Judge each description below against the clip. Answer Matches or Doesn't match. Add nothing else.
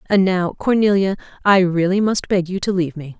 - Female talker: Matches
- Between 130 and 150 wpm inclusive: Doesn't match